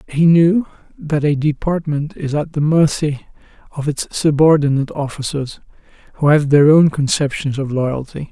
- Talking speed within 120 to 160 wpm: Yes, average, 145 wpm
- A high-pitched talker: No, medium, 150 Hz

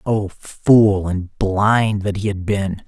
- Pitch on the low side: Yes, low, 100 Hz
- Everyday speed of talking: Yes, average, 165 wpm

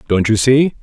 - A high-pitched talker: No, low, 115 Hz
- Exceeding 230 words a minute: No, fast, 220 wpm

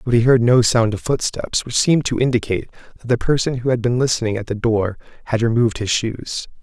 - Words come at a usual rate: No, fast, 225 wpm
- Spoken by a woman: No, male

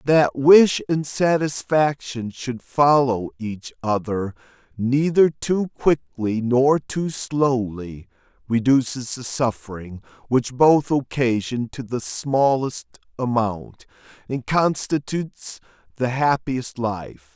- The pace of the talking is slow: Yes, slow, 100 wpm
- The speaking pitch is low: Yes, low, 130 Hz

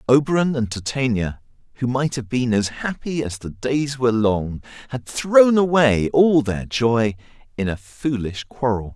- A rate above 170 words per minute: No, average, 160 wpm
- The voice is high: No, low, 125 Hz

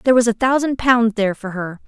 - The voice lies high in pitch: Yes, high, 230 Hz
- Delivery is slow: No, fast, 255 wpm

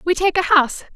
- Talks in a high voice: Yes, very high, 340 Hz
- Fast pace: Yes, fast, 250 wpm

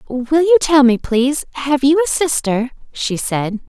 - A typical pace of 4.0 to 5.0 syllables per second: Yes, 4.3 syllables/s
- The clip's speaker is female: Yes, female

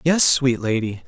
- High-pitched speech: No, low, 130 Hz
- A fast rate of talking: No, average, 165 wpm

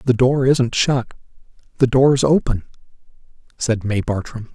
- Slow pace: Yes, slow, 130 wpm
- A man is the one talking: Yes, male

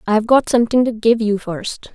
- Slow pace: No, fast, 215 wpm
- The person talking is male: No, female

